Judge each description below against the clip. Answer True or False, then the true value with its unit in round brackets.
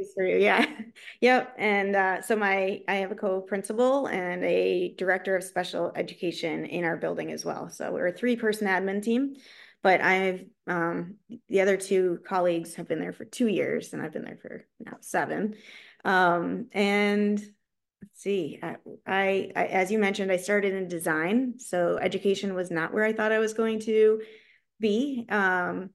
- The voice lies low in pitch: False (195 Hz)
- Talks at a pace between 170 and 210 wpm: True (180 wpm)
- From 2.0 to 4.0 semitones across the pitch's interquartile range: True (2.9 semitones)